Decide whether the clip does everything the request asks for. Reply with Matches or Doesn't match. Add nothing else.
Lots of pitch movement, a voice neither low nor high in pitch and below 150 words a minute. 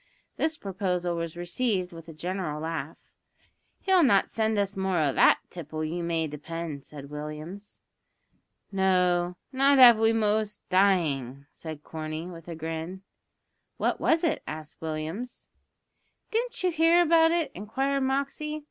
Matches